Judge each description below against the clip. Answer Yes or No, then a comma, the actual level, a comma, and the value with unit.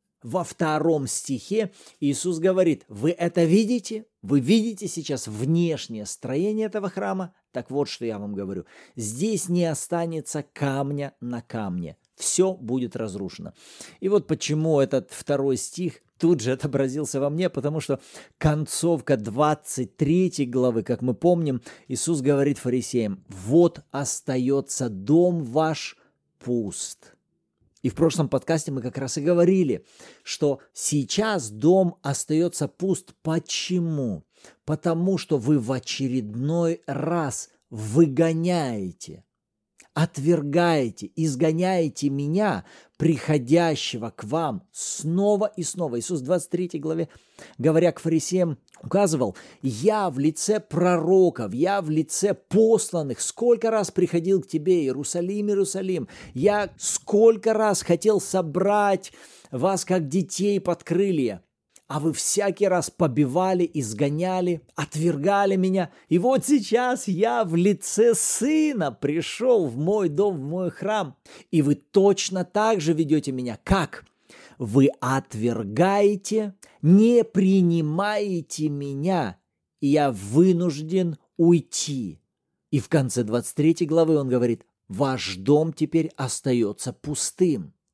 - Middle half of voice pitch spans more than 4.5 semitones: Yes, average, 5.2 semitones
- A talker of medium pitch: Yes, medium, 160 Hz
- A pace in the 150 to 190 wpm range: No, average, 115 wpm